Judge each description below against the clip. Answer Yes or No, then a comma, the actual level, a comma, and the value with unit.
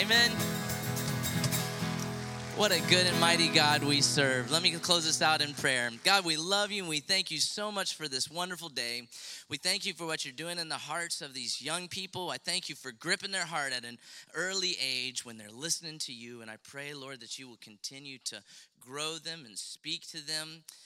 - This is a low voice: No, medium, 155 Hz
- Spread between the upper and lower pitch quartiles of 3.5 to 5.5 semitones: Yes, average, 4.7 semitones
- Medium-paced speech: No, fast, 215 wpm